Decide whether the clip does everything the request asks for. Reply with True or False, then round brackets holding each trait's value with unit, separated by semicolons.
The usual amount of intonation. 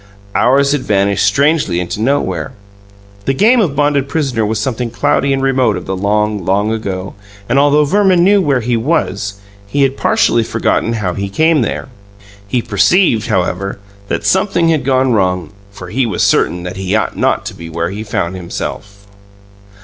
False (6.0 semitones)